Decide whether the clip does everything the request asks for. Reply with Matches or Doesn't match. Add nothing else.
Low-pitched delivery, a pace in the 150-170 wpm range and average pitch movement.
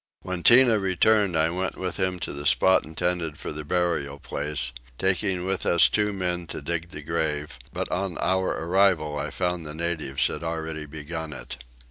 Doesn't match